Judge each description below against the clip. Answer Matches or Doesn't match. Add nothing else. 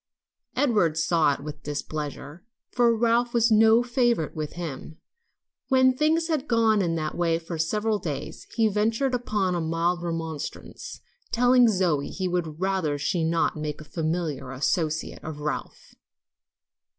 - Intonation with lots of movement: Matches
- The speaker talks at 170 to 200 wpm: Doesn't match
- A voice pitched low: Doesn't match